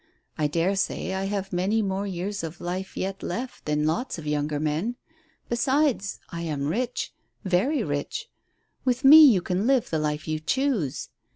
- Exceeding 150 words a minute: Yes, average, 170 wpm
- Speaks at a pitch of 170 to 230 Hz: Yes, high, 190 Hz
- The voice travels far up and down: Yes, wide, 7.1 semitones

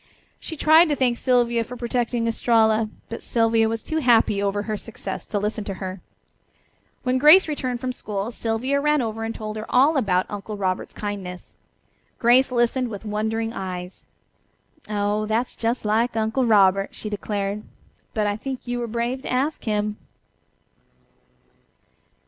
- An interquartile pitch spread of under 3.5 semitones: Yes, average, 3.0 semitones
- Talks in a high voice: Yes, high, 225 Hz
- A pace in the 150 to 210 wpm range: Yes, average, 160 wpm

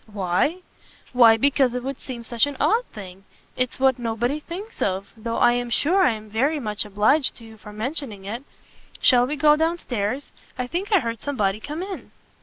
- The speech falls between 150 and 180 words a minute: No, average, 200 wpm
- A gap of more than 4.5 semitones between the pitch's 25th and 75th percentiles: Yes, average, 5.0 semitones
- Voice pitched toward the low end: No, high, 245 Hz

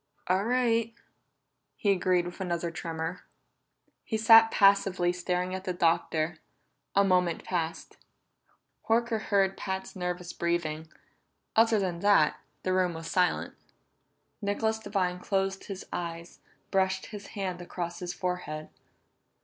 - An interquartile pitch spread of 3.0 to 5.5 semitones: No, narrow, 2.4 semitones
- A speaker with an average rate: No, slow, 125 wpm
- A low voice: No, medium, 185 Hz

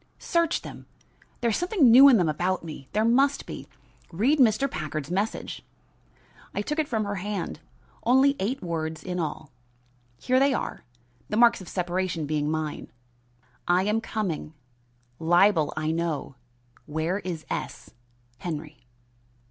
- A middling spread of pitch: No, wide, 6.7 semitones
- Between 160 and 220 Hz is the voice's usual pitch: Yes, medium, 185 Hz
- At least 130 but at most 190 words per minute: Yes, average, 145 wpm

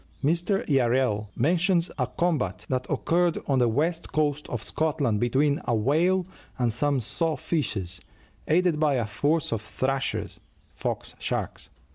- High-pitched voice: No, medium, 140 Hz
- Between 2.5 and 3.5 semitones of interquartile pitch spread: No, wide, 5.4 semitones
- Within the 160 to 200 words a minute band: No, average, 140 wpm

